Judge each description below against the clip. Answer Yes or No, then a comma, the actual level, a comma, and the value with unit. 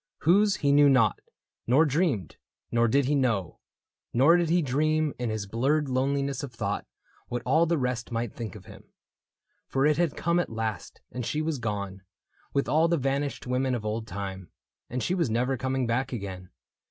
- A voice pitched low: Yes, low, 130 Hz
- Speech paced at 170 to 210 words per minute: Yes, average, 190 wpm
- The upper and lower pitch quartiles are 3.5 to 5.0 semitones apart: Yes, average, 4.5 semitones